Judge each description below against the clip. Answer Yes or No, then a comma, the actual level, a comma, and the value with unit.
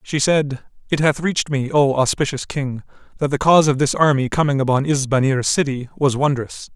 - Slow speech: No, average, 185 wpm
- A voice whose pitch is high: No, medium, 140 Hz